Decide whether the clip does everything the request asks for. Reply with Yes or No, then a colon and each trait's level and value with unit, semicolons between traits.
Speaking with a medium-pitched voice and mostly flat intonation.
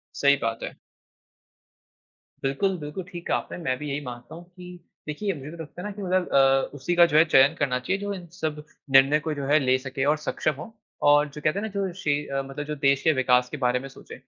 No: medium, 150 Hz; average, 4.3 semitones